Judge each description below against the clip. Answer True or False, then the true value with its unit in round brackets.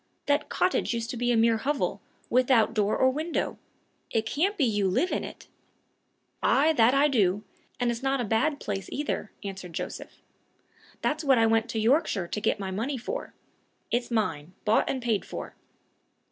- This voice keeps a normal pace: True (180 wpm)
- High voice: True (235 Hz)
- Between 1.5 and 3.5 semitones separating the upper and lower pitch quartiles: False (4.4 semitones)